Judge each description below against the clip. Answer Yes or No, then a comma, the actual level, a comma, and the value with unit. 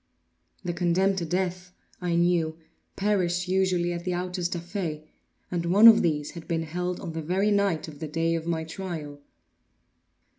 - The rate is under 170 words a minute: No, average, 175 wpm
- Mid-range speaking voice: Yes, medium, 175 Hz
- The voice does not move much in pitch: Yes, narrow, 1.9 semitones